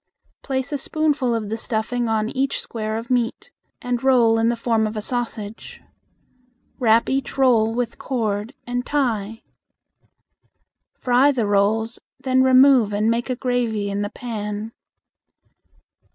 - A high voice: Yes, high, 235 Hz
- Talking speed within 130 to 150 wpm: Yes, average, 140 wpm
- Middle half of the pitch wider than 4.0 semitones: No, average, 2.7 semitones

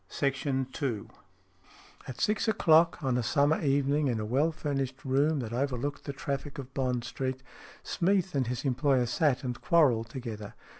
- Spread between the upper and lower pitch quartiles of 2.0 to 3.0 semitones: Yes, average, 2.7 semitones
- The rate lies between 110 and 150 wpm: No, average, 165 wpm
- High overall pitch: No, low, 135 Hz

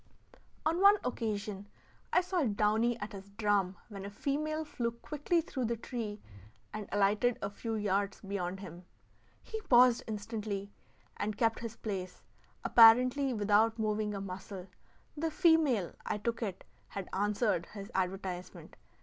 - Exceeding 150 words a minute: No, average, 140 wpm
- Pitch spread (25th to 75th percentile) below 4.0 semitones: Yes, average, 3.4 semitones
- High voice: Yes, high, 215 Hz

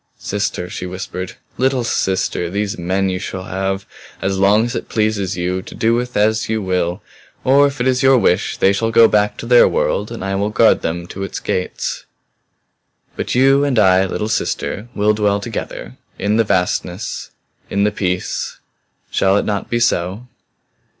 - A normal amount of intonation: Yes, average, 3.5 semitones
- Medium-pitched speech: No, low, 100 Hz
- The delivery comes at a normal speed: Yes, average, 180 wpm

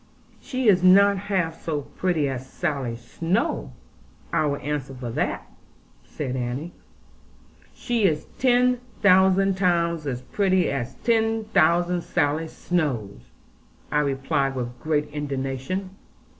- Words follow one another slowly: Yes, slow, 120 wpm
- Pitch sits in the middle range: Yes, medium, 160 Hz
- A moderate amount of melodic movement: No, wide, 5.8 semitones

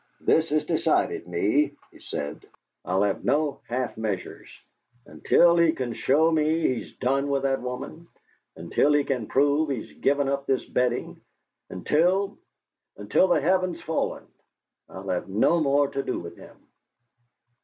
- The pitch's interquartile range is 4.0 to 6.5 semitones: Yes, average, 4.4 semitones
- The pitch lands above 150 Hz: No, medium, 140 Hz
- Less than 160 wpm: Yes, average, 145 wpm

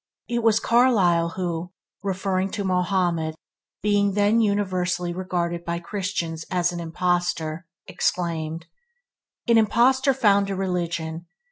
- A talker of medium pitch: Yes, medium, 180 Hz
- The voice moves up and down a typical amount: Yes, average, 3.0 semitones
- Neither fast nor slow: No, slow, 115 wpm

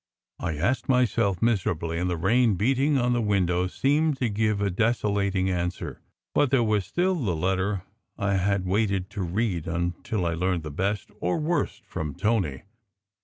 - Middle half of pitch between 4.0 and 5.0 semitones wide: Yes, average, 4.6 semitones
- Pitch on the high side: No, low, 100 Hz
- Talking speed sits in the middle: Yes, average, 170 wpm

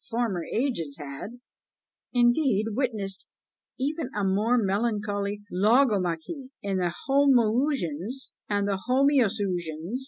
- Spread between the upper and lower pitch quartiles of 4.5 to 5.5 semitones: Yes, average, 4.9 semitones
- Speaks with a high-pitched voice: Yes, high, 215 Hz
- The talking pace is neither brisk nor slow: No, slow, 95 wpm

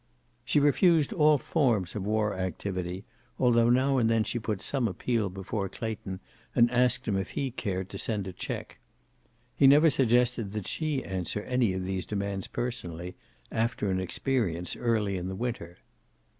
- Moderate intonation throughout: Yes, average, 4.8 semitones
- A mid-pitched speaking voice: No, low, 110 Hz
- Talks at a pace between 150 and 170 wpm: Yes, average, 165 wpm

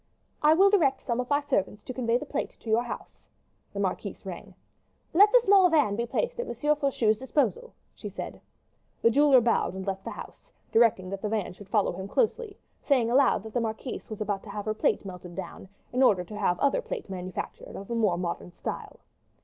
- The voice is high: Yes, high, 230 Hz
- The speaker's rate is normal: No, fast, 215 wpm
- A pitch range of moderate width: No, wide, 6.4 semitones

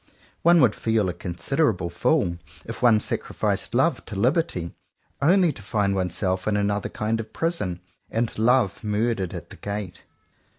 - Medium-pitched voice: No, low, 105 Hz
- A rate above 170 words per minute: No, average, 155 wpm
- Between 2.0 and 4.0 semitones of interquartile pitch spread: No, average, 4.9 semitones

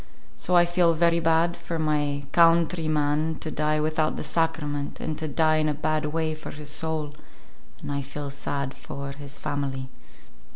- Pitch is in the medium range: Yes, medium, 155 Hz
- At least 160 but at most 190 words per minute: Yes, average, 175 wpm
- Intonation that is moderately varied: No, narrow, 1.9 semitones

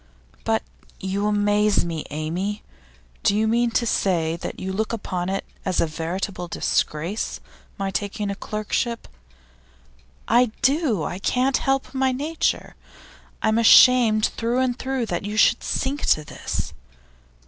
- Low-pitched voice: No, high, 210 Hz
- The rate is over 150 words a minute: No, average, 145 wpm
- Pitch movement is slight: No, average, 4.3 semitones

